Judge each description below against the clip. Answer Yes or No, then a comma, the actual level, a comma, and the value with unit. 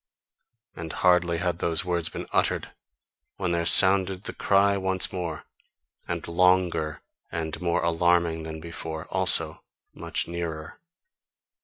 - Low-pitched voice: Yes, very low, 85 Hz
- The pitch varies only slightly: Yes, narrow, 1.9 semitones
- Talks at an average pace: No, slow, 125 wpm